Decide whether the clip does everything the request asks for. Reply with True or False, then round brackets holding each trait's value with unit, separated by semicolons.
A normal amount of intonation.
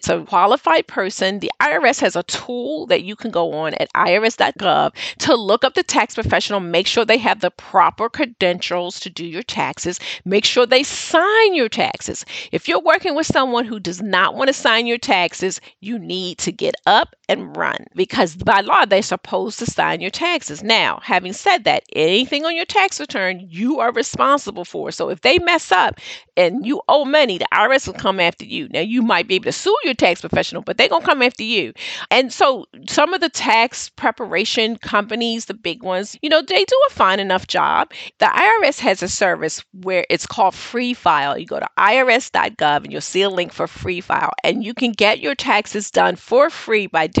False (7.4 semitones)